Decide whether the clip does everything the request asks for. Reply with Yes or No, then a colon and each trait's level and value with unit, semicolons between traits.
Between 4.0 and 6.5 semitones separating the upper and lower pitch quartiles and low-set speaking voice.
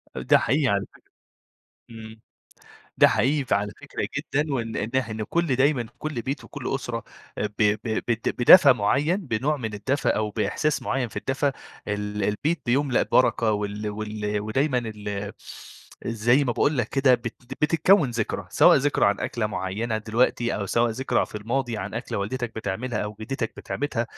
Yes: average, 4.3 semitones; low, 115 Hz